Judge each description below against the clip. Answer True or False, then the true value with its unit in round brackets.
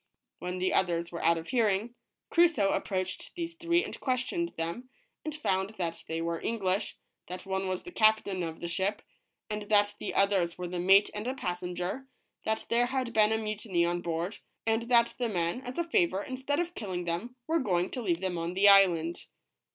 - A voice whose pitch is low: False (195 Hz)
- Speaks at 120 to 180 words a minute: False (200 wpm)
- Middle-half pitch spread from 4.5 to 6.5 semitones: True (5.4 semitones)